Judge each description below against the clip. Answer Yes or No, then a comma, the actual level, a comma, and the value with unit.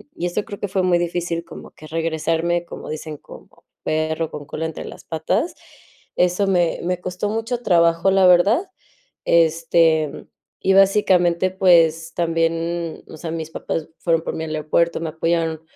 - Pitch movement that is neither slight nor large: No, narrow, 1.9 semitones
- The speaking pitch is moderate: Yes, medium, 170 Hz